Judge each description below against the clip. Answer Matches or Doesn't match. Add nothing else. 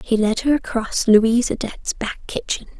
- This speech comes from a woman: Matches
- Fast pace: Doesn't match